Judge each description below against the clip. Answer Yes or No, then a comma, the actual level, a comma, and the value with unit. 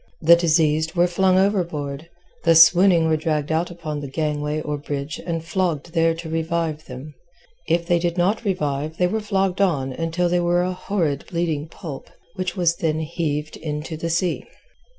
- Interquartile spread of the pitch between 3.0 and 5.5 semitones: No, narrow, 2.4 semitones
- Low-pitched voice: No, medium, 165 Hz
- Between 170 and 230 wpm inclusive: Yes, average, 175 wpm